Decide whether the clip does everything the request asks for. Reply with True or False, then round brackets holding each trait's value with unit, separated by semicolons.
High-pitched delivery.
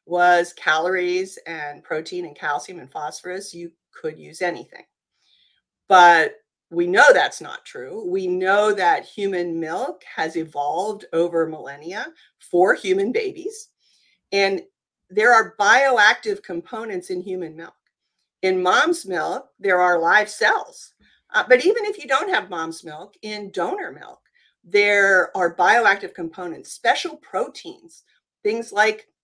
True (200 Hz)